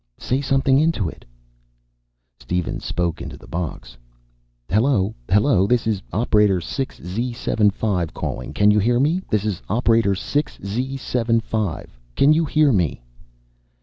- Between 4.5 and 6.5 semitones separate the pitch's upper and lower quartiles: Yes, average, 5.3 semitones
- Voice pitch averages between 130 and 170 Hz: No, low, 110 Hz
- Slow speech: Yes, slow, 130 wpm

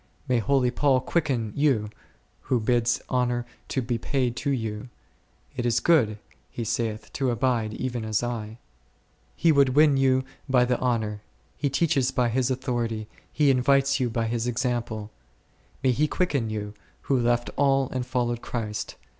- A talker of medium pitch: No, low, 125 Hz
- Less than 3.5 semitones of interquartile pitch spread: Yes, average, 2.7 semitones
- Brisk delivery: No, average, 160 wpm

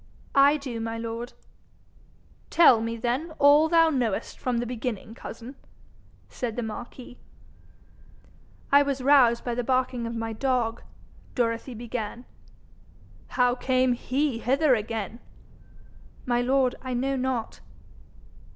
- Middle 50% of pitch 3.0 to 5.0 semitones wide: No, narrow, 2.5 semitones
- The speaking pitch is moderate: No, high, 245 Hz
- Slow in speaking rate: Yes, slow, 125 wpm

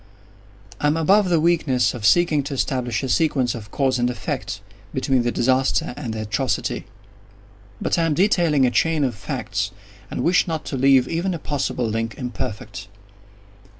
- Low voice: Yes, low, 130 Hz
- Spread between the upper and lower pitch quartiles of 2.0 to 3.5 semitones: No, average, 4.9 semitones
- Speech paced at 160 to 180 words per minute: Yes, average, 165 wpm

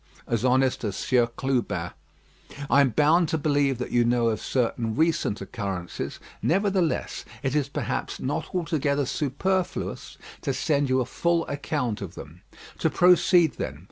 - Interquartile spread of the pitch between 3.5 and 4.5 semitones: No, average, 4.9 semitones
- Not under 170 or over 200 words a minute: No, average, 150 wpm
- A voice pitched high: No, medium, 140 Hz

